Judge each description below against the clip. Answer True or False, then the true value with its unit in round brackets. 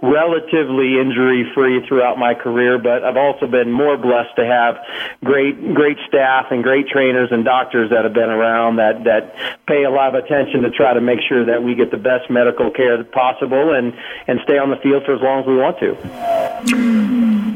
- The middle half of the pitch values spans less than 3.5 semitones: True (2.5 semitones)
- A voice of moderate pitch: False (130 Hz)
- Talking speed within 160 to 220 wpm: True (200 wpm)